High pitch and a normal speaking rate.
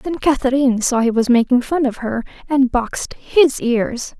Yes: very high, 255 Hz; average, 185 wpm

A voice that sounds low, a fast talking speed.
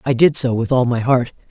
Yes: low, 125 Hz; fast, 280 wpm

